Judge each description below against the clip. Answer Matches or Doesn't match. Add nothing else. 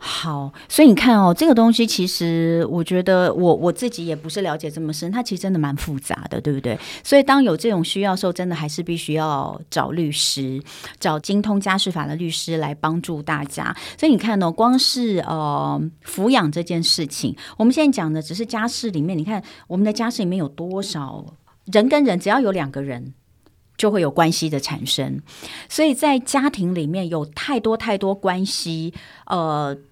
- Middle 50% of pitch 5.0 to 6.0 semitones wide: Matches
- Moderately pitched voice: Matches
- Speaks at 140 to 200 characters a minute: Doesn't match